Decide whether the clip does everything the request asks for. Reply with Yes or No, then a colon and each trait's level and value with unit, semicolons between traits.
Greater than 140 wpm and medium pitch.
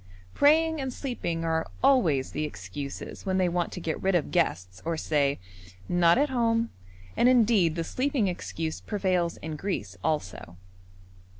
Yes: average, 155 wpm; medium, 175 Hz